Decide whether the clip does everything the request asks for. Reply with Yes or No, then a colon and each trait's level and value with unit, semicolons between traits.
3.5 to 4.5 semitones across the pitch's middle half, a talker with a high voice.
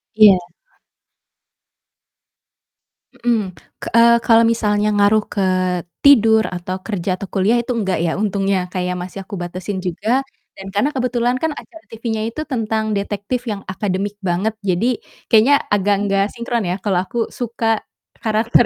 No: average, 3.1 semitones; high, 210 Hz